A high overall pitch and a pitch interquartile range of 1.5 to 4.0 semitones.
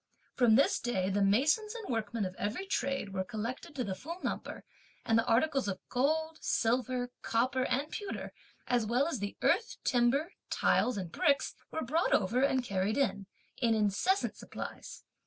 No: high, 245 Hz; average, 5.1 semitones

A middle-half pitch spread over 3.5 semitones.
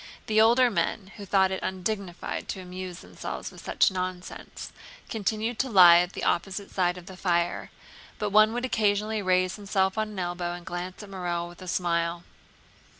No: average, 2.9 semitones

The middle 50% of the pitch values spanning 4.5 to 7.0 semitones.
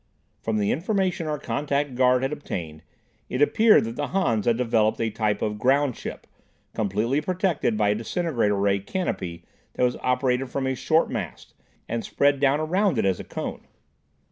Yes: wide, 5.5 semitones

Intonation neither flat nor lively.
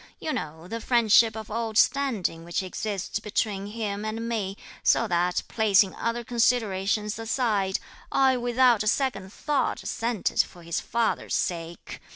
Yes: average, 3.4 semitones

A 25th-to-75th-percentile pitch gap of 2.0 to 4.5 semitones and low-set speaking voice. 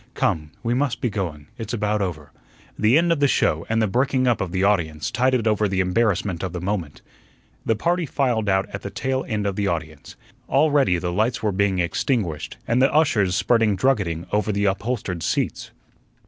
No: average, 5.0 semitones; low, 105 Hz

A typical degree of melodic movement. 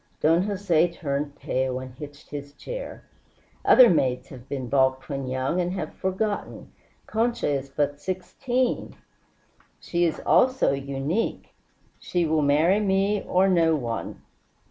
No: wide, 5.7 semitones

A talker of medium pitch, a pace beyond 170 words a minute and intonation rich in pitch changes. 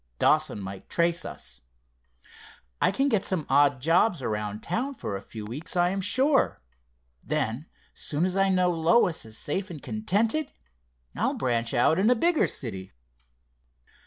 No: medium, 170 Hz; average, 155 wpm; wide, 9.0 semitones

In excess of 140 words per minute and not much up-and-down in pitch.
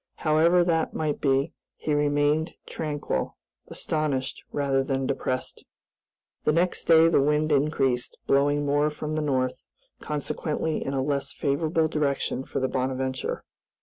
No: slow, 135 wpm; narrow, 2.3 semitones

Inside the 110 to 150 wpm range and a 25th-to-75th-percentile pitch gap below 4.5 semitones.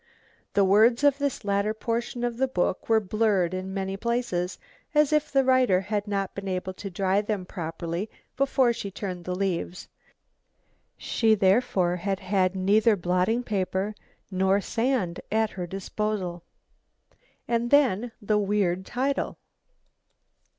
Yes: average, 140 wpm; average, 3.8 semitones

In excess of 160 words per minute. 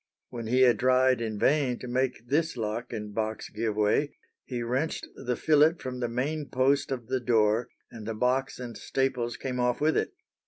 Yes: average, 195 wpm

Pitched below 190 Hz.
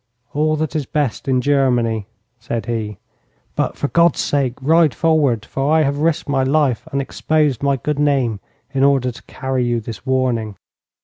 Yes: low, 135 Hz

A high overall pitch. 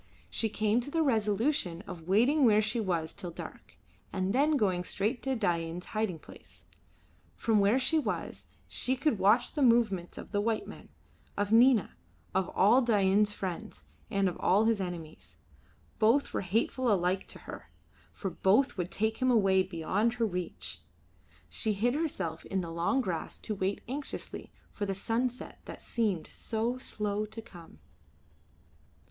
Yes: high, 210 Hz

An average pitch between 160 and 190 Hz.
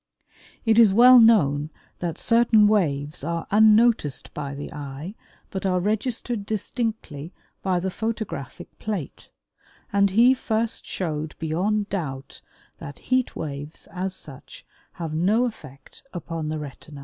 Yes: medium, 185 Hz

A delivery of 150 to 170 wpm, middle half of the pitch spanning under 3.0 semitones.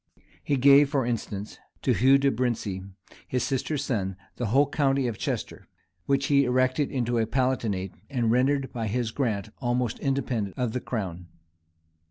No: average, 160 wpm; average, 3.5 semitones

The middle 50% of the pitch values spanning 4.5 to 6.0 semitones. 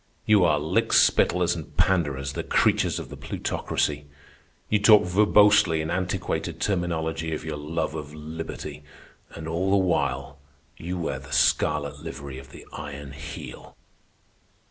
No: average, 3.6 semitones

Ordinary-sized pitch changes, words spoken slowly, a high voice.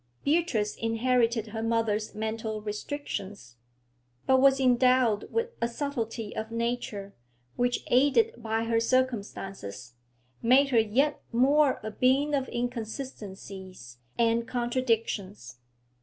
Yes: average, 3.2 semitones; slow, 110 wpm; high, 230 Hz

